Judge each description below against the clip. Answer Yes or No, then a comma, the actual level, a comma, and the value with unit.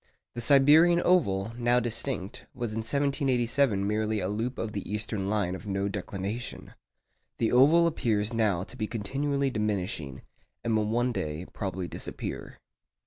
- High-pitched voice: No, low, 110 Hz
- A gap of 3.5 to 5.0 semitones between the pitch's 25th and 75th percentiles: Yes, average, 3.9 semitones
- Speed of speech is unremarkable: Yes, average, 145 wpm